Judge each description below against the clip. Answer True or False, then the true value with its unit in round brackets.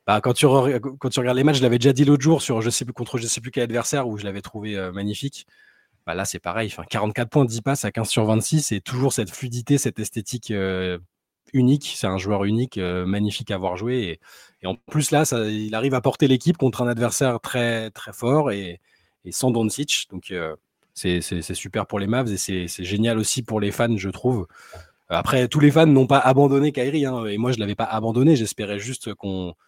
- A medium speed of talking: False (245 wpm)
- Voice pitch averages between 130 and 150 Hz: False (115 Hz)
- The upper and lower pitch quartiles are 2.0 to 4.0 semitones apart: False (4.4 semitones)